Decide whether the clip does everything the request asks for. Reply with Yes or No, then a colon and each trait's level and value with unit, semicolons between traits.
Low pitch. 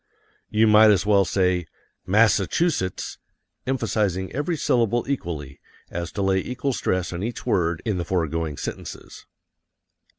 Yes: very low, 95 Hz